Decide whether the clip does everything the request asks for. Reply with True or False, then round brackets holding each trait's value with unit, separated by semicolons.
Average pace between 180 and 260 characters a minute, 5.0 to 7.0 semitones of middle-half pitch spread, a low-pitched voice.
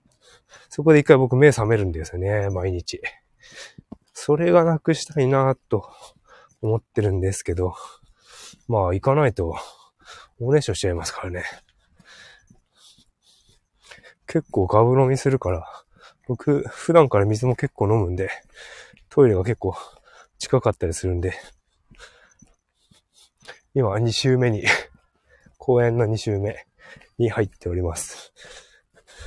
True (235 characters per minute; 5.7 semitones; 115 Hz)